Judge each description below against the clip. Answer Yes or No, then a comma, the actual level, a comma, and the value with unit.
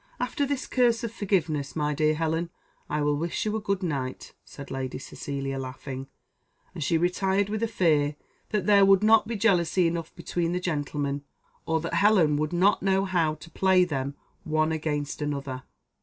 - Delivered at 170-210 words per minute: Yes, average, 180 wpm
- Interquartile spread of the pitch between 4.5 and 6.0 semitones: Yes, average, 4.9 semitones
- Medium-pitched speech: Yes, medium, 165 Hz